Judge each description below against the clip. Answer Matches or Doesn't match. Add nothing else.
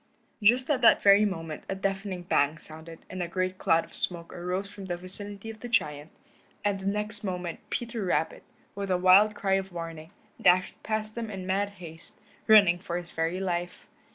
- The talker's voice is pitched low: Doesn't match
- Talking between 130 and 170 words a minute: Doesn't match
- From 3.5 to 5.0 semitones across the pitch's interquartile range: Doesn't match